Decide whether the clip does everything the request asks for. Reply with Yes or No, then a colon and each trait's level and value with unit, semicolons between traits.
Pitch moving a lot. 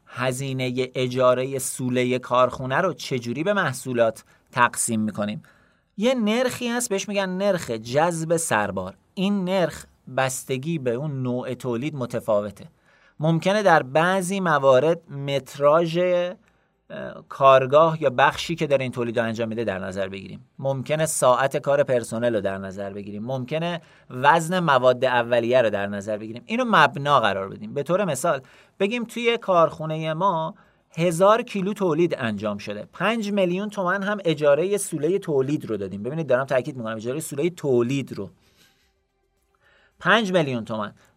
Yes: wide, 6.7 semitones